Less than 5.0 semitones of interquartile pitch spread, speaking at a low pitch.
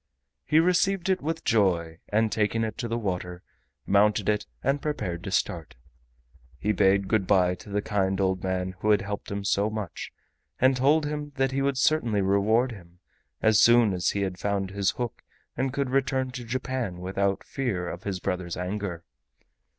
No: average, 5.3 semitones; low, 105 Hz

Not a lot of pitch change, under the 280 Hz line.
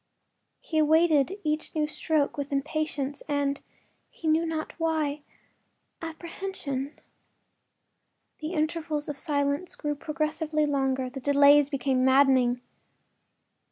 No: narrow, 2.0 semitones; very high, 295 Hz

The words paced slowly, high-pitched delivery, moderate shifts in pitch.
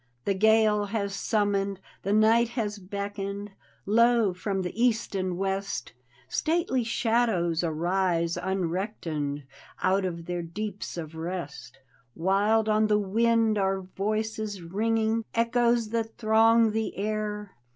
Yes: slow, 120 wpm; high, 205 Hz; average, 3.0 semitones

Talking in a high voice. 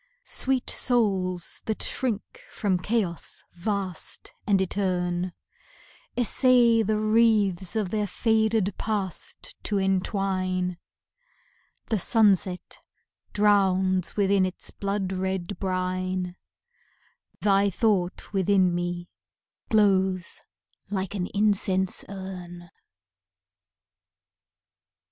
Yes: high, 195 Hz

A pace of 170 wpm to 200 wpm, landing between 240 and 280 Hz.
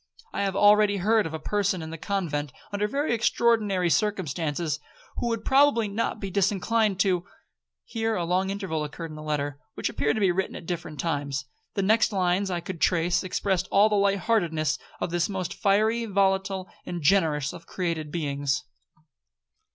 No: average, 180 wpm; high, 190 Hz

